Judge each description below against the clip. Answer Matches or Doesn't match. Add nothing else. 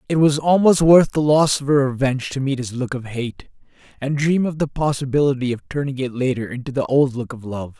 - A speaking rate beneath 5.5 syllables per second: Doesn't match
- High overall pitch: Doesn't match